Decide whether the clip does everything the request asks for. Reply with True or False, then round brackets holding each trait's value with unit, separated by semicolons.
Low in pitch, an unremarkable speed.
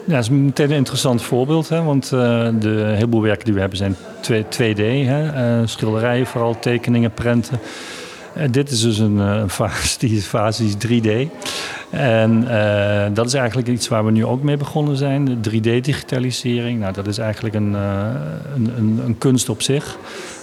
True (115 Hz; 190 wpm)